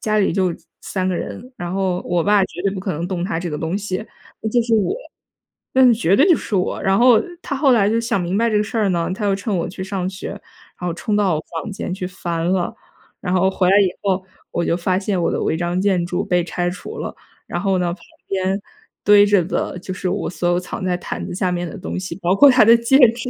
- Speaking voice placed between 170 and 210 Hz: Yes, high, 190 Hz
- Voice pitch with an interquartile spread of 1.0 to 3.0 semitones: Yes, average, 2.7 semitones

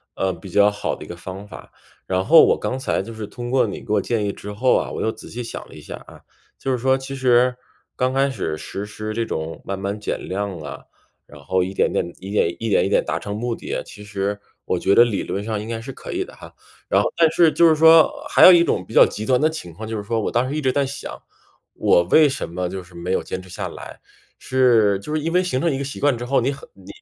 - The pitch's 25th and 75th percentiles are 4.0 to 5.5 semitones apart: Yes, average, 5.2 semitones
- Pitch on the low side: Yes, low, 115 Hz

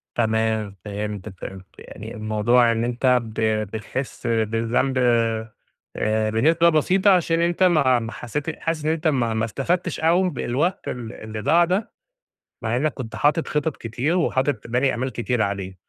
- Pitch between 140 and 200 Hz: No, low, 125 Hz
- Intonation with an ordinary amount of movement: No, wide, 6.1 semitones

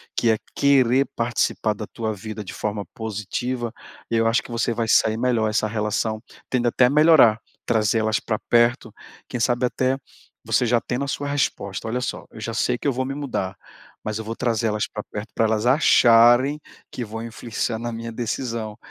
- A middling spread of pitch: No, narrow, 2.2 semitones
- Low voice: Yes, low, 115 Hz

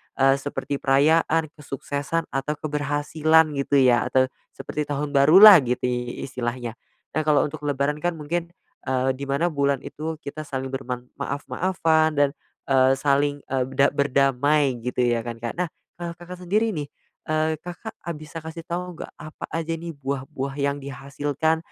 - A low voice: No, medium, 145 Hz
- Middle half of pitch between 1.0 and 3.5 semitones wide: Yes, average, 2.8 semitones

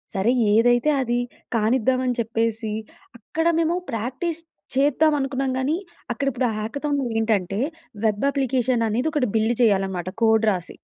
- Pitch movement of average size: Yes, average, 3.6 semitones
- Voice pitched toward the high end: Yes, high, 240 Hz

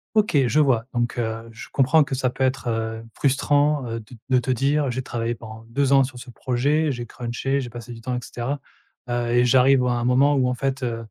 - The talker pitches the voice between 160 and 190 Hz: No, low, 125 Hz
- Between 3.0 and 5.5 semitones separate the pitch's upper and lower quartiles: No, narrow, 2.5 semitones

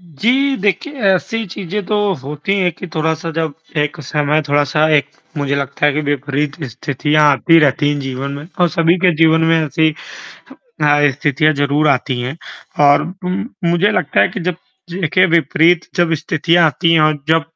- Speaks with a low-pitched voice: No, medium, 155 Hz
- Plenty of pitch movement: No, average, 3.1 semitones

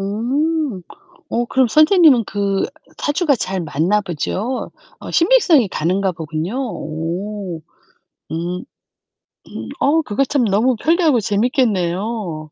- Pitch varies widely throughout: Yes, wide, 7.0 semitones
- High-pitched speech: Yes, high, 210 Hz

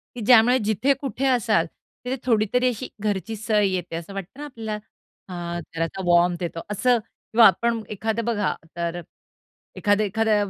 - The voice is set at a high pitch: Yes, high, 215 Hz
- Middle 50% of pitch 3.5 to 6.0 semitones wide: Yes, average, 4.0 semitones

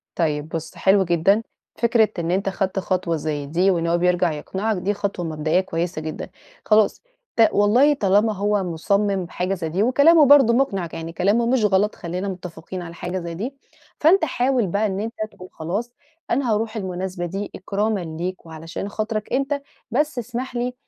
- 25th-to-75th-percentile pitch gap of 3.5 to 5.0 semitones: Yes, average, 4.5 semitones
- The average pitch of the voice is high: Yes, high, 195 Hz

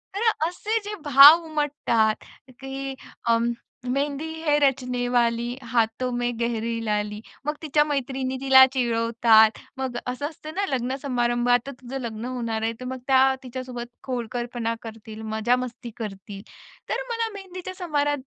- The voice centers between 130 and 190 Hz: No, very high, 250 Hz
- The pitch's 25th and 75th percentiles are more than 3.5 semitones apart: No, average, 3.2 semitones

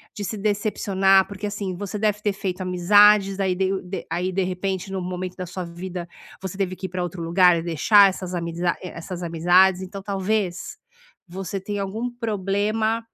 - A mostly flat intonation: Yes, narrow, 2.0 semitones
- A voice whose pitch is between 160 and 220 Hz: Yes, high, 190 Hz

